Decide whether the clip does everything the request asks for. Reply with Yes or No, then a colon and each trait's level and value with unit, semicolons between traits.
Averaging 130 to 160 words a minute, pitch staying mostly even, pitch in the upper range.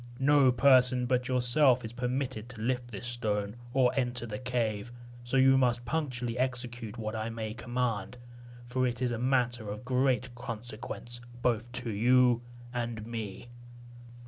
No: average, 150 wpm; narrow, 1.7 semitones; low, 120 Hz